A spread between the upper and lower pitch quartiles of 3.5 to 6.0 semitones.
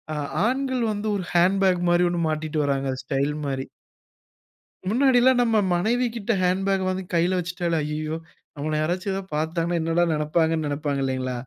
Yes: average, 4.2 semitones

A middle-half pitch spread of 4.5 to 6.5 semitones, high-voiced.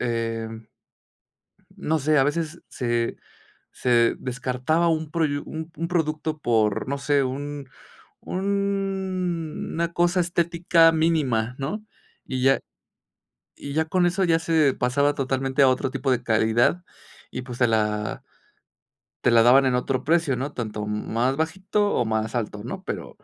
No: average, 5.1 semitones; medium, 140 Hz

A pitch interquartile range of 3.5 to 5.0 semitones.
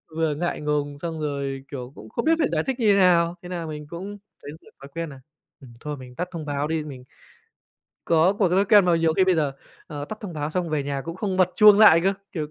Yes: average, 4.1 semitones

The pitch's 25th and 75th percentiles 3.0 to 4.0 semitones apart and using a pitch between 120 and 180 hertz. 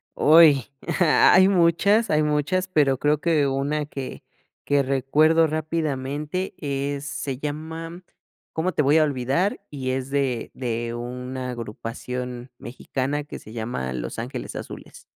Yes: average, 3.6 semitones; medium, 140 Hz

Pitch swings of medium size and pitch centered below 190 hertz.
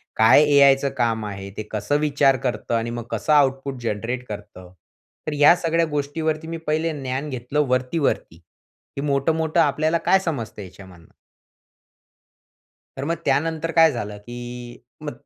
Yes: average, 5.0 semitones; low, 135 Hz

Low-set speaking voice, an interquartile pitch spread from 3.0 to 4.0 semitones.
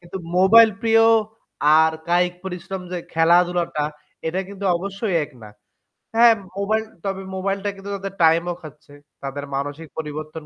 No: medium, 180 Hz; average, 3.6 semitones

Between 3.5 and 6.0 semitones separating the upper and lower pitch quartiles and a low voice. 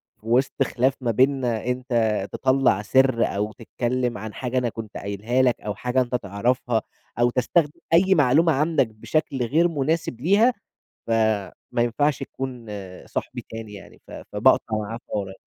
No: average, 3.1 semitones; low, 125 Hz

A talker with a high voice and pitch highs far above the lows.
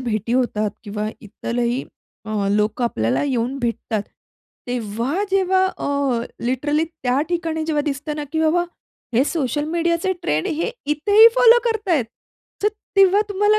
Yes: very high, 290 Hz; wide, 6.6 semitones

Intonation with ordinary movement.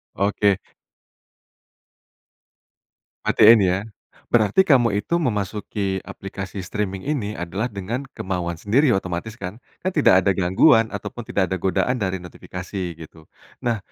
Yes: average, 3.6 semitones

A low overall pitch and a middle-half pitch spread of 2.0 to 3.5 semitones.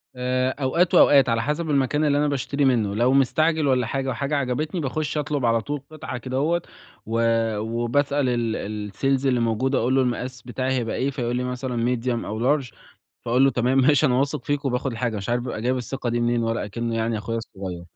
Yes: low, 125 Hz; average, 3.0 semitones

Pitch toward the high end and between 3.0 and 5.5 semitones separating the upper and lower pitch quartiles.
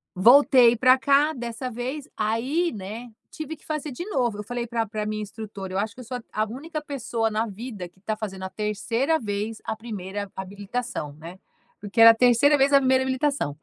Yes: high, 230 Hz; average, 4.0 semitones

